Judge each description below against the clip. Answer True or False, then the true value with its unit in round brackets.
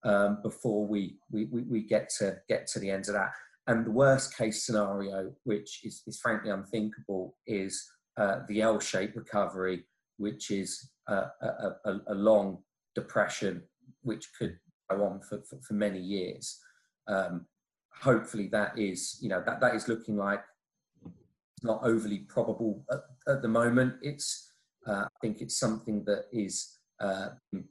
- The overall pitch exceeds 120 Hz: False (105 Hz)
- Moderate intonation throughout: False (2.3 semitones)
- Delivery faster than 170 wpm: False (160 wpm)